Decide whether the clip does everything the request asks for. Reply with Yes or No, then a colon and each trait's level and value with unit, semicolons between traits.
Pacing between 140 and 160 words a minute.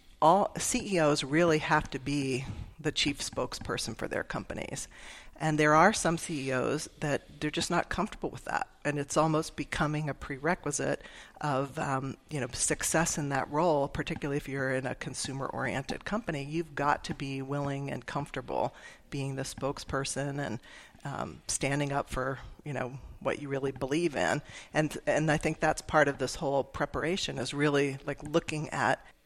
No: average, 180 wpm